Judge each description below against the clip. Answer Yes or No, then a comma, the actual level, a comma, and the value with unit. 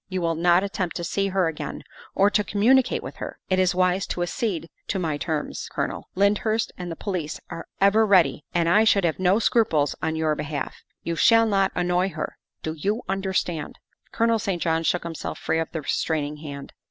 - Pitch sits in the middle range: Yes, medium, 180 Hz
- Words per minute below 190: No, average, 200 wpm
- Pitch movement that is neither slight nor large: Yes, average, 3.6 semitones